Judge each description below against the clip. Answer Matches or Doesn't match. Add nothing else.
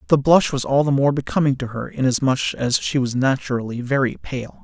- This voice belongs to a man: Matches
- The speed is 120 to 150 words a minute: Doesn't match